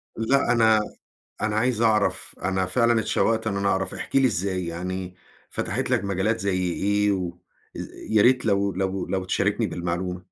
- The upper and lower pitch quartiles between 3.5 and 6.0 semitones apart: No, average, 3.1 semitones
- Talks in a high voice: No, low, 100 Hz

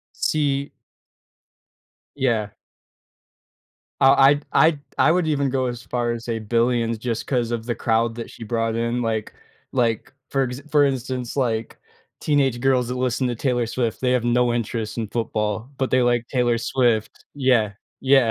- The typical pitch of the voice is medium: No, low, 120 Hz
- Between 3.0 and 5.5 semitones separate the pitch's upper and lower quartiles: No, narrow, 2.4 semitones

